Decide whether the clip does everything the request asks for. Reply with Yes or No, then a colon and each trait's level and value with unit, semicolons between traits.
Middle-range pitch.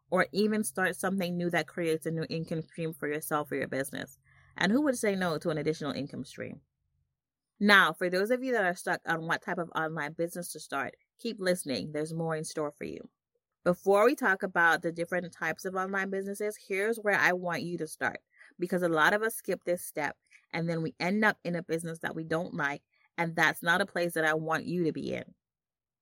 Yes: medium, 175 Hz